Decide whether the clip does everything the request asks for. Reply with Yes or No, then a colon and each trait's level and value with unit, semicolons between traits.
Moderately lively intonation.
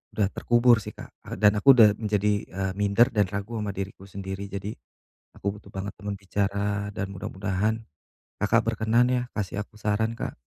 No: narrow, 1.7 semitones